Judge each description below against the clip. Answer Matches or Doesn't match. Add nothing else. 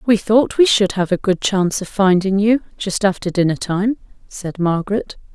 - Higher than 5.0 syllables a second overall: Doesn't match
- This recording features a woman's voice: Matches